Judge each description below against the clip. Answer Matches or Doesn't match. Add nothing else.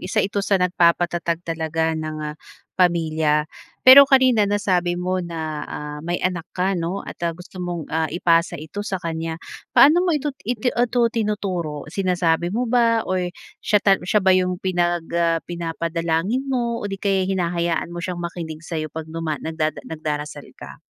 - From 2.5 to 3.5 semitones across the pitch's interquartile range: Matches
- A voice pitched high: Doesn't match